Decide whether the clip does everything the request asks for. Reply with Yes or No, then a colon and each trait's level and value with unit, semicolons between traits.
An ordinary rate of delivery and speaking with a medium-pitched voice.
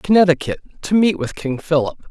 Yes: average, 170 wpm; medium, 165 Hz